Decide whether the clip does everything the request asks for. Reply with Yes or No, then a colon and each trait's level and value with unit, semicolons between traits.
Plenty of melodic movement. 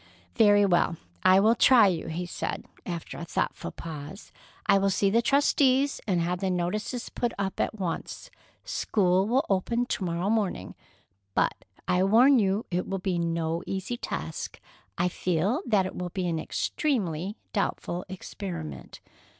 No: average, 3.8 semitones